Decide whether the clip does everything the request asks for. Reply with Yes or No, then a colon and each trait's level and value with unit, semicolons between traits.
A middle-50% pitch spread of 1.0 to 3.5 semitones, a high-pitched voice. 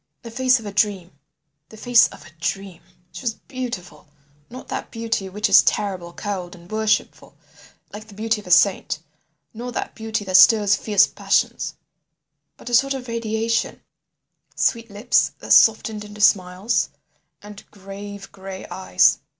Yes: average, 3.0 semitones; high, 210 Hz